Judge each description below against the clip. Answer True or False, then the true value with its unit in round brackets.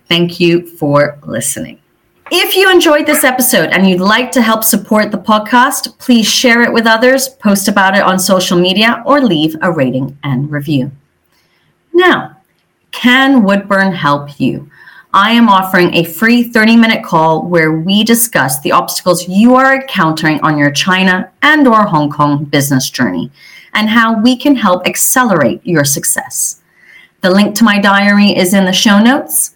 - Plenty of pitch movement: True (5.7 semitones)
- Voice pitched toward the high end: True (200 Hz)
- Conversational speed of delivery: True (165 wpm)